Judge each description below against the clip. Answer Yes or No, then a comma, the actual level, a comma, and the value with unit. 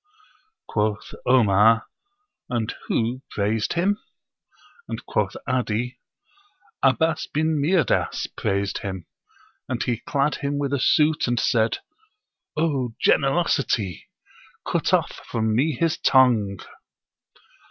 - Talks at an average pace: No, slow, 105 wpm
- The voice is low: Yes, low, 125 Hz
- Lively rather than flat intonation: No, average, 4.8 semitones